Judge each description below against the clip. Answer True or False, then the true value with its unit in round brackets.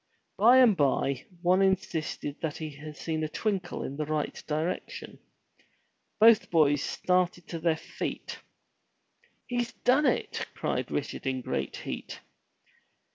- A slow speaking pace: True (130 wpm)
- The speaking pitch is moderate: True (165 Hz)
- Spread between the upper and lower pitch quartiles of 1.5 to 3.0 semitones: False (4.4 semitones)